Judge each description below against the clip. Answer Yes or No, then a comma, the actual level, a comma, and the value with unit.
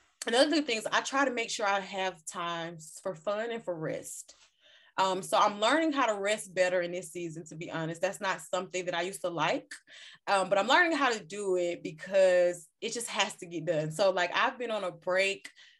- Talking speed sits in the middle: No, fast, 230 wpm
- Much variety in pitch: No, average, 3.7 semitones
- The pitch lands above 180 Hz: Yes, high, 190 Hz